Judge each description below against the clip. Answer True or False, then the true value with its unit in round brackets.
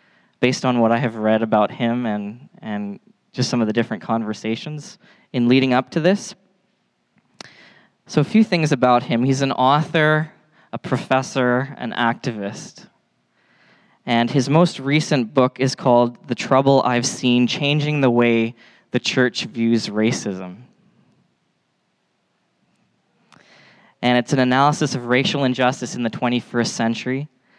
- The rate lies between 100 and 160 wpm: True (135 wpm)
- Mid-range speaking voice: False (125 Hz)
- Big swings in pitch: False (3.6 semitones)